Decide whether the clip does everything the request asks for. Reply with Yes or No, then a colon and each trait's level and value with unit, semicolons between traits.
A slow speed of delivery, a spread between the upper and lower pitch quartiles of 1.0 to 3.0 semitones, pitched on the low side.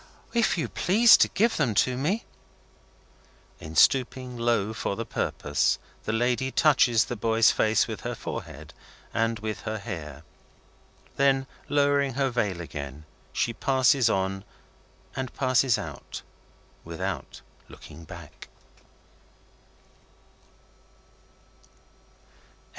No: slow, 110 wpm; wide, 5.4 semitones; low, 115 Hz